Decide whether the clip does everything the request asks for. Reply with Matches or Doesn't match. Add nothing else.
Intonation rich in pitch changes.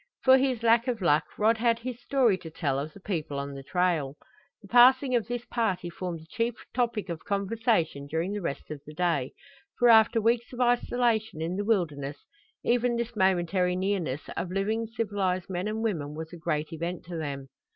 Matches